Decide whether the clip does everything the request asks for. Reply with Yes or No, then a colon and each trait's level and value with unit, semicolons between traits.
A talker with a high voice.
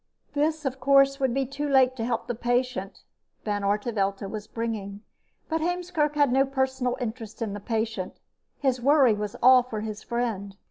Yes: high, 245 Hz